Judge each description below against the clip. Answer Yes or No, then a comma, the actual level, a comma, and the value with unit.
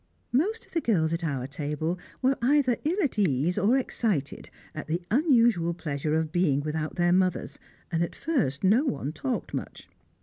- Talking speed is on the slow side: No, average, 175 wpm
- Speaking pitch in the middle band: Yes, medium, 175 Hz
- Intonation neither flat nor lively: No, wide, 7.6 semitones